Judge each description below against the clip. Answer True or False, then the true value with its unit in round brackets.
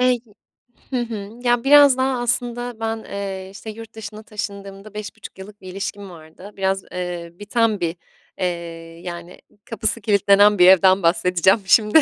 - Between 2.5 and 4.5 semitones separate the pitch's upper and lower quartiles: True (3.1 semitones)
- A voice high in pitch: True (200 Hz)